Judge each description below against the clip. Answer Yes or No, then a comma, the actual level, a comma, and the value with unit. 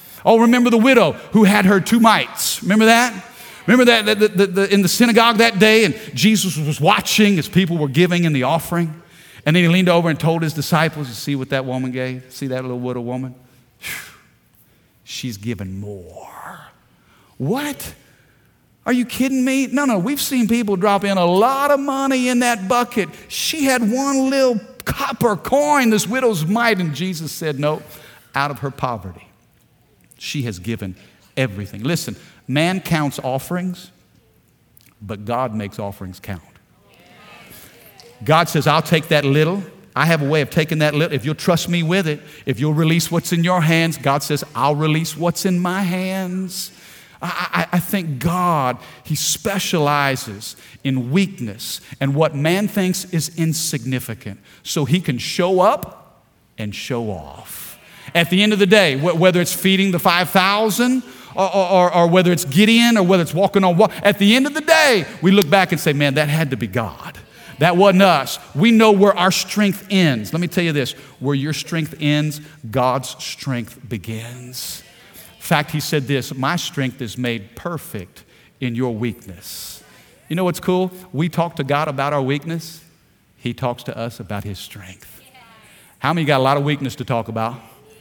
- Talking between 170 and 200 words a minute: Yes, average, 180 wpm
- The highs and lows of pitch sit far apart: Yes, wide, 6.7 semitones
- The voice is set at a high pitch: No, medium, 160 Hz